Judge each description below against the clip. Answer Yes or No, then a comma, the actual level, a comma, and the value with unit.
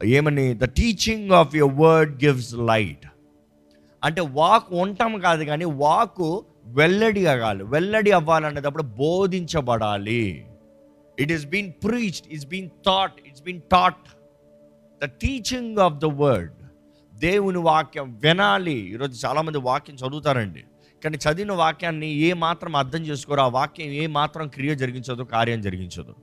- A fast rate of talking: Yes, fast, 130 wpm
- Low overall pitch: No, medium, 150 Hz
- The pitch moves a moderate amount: No, wide, 5.8 semitones